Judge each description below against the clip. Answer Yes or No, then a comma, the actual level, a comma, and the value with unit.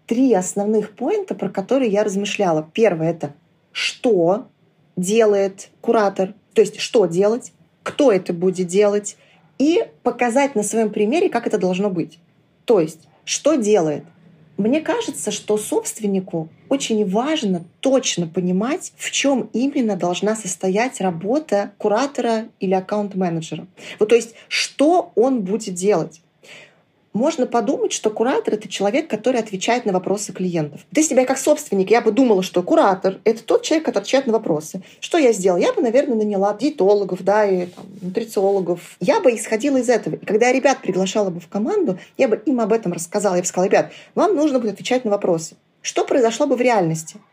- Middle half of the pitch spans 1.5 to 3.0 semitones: No, average, 4.5 semitones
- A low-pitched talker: No, high, 205 Hz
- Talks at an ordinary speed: No, fast, 165 wpm